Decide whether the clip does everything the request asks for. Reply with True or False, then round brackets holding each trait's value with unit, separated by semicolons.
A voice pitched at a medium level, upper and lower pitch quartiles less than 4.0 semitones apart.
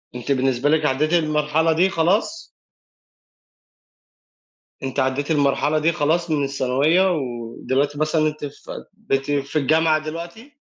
True (150 Hz; 2.9 semitones)